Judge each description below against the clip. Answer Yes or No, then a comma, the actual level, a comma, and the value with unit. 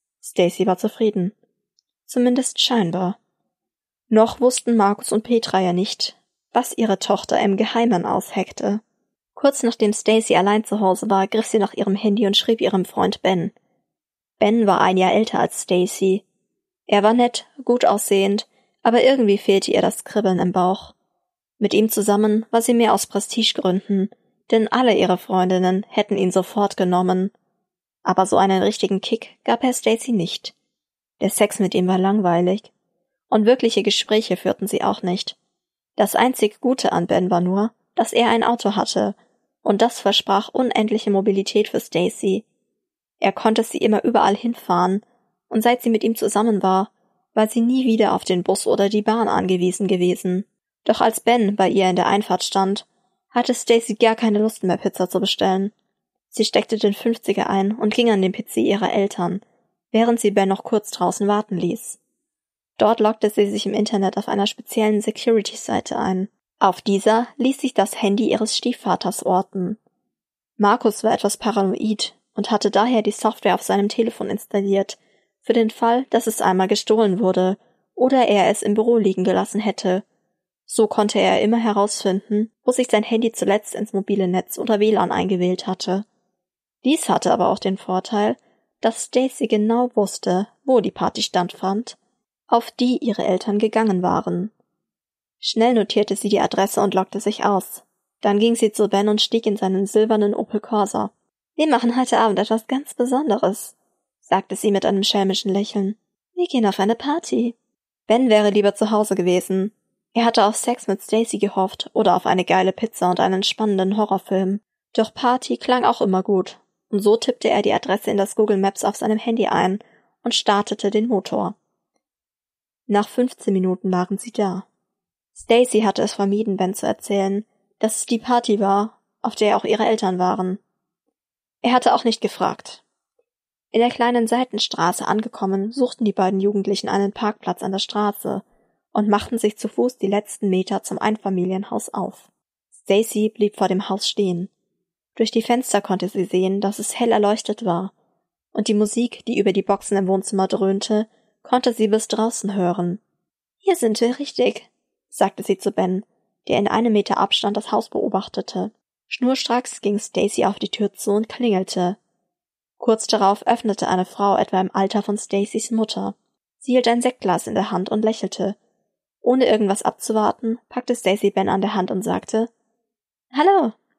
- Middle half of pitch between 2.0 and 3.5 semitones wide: Yes, average, 3.0 semitones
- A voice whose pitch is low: No, high, 210 Hz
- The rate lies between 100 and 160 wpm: No, average, 170 wpm